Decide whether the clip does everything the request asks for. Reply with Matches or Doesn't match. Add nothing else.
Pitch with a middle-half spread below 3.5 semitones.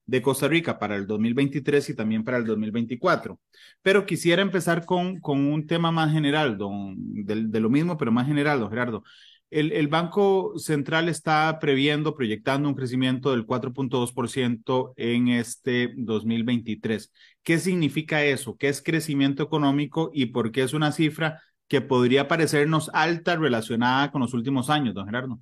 Doesn't match